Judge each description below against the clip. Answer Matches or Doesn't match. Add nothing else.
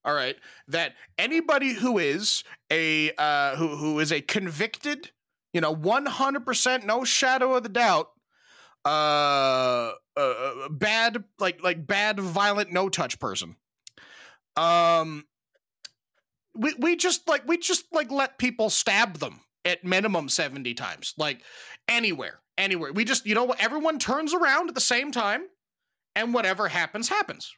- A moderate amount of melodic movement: Doesn't match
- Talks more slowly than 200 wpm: Matches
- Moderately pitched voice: Doesn't match